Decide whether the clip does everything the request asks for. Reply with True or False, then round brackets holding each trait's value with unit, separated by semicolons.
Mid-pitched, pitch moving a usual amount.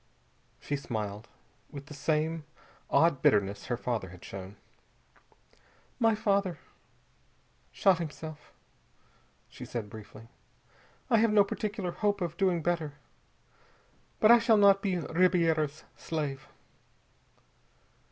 False (160 Hz; 6.9 semitones)